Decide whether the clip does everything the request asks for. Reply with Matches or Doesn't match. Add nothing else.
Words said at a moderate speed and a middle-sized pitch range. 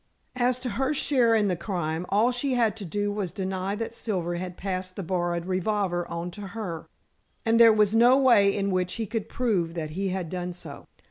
Doesn't match